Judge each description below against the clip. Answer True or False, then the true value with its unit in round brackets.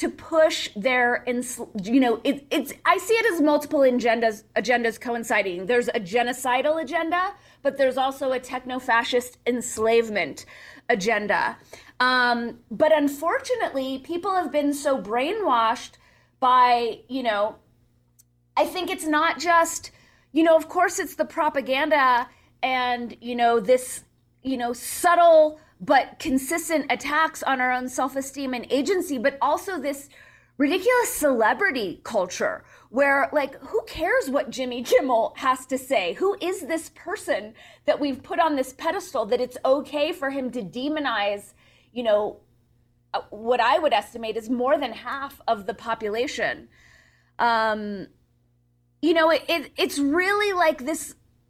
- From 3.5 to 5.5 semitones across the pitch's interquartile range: True (4.8 semitones)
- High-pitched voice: True (265 Hz)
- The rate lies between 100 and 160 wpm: True (140 wpm)